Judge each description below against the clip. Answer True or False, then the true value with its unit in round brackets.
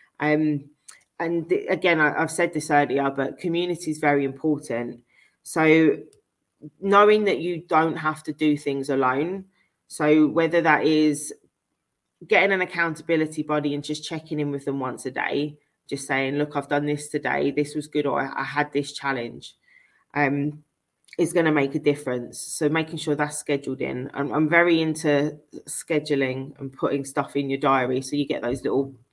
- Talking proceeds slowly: False (175 wpm)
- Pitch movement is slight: True (1.9 semitones)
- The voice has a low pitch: False (150 Hz)